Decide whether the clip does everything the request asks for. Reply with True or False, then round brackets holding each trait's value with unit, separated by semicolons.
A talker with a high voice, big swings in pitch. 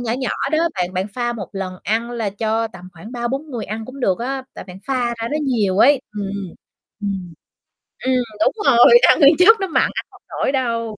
False (230 Hz; 4.6 semitones)